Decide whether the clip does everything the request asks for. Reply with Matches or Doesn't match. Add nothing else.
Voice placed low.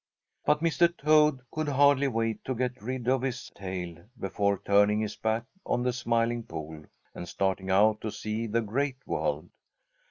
Matches